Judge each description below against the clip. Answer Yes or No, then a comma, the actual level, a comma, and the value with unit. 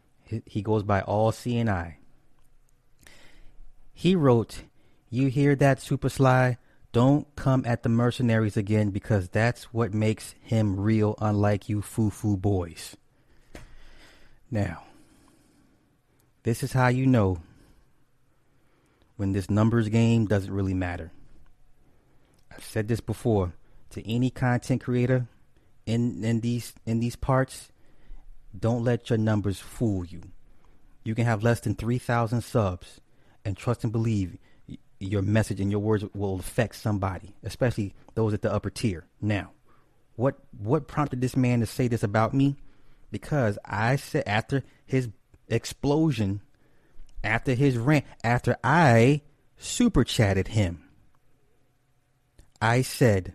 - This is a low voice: Yes, low, 115 Hz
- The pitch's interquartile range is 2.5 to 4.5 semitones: Yes, average, 3.7 semitones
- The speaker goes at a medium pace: No, slow, 130 wpm